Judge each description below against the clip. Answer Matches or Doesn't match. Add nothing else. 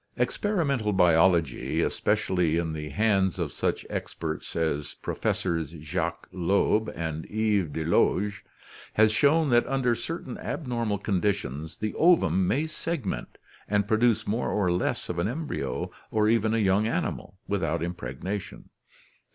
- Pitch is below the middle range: Matches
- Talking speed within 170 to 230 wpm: Doesn't match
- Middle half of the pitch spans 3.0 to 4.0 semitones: Doesn't match